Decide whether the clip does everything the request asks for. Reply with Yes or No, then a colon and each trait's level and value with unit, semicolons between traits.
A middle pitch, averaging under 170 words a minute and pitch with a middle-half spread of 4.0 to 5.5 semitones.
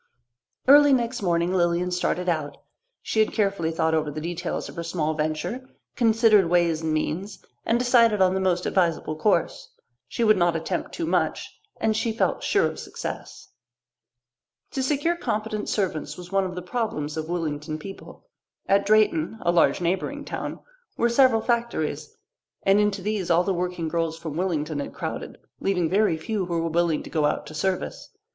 No: medium, 180 Hz; average, 175 wpm; average, 4.7 semitones